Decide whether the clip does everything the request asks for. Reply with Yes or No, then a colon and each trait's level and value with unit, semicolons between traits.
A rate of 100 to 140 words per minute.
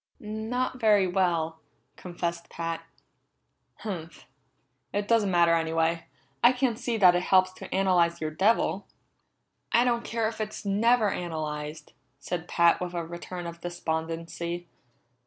Yes: slow, 135 wpm